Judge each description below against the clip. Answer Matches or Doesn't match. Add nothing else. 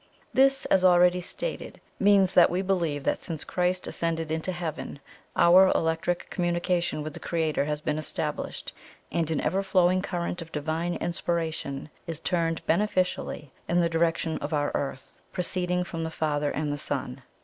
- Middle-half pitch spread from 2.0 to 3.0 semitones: Matches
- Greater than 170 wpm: Doesn't match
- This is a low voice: Doesn't match